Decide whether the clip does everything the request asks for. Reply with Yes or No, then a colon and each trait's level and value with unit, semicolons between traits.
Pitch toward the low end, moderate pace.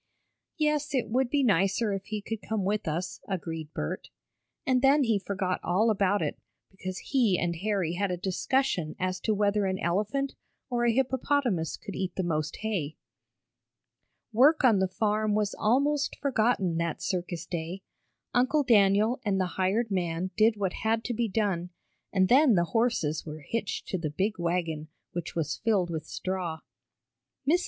No: high, 200 Hz; average, 170 wpm